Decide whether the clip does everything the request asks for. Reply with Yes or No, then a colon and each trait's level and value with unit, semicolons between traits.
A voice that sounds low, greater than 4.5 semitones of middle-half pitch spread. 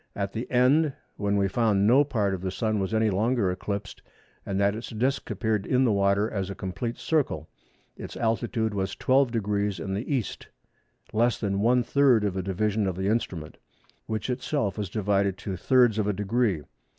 No: low, 105 Hz; average, 3.2 semitones